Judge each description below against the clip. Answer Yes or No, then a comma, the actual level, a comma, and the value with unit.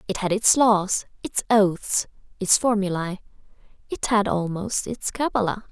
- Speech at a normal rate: No, slow, 125 wpm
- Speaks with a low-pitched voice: No, high, 200 Hz